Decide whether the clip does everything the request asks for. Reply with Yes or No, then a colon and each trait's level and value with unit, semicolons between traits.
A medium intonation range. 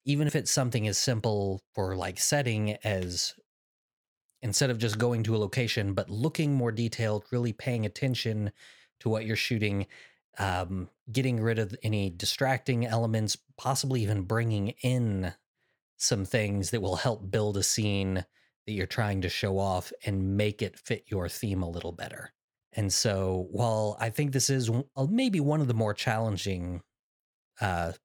Yes: average, 3.7 semitones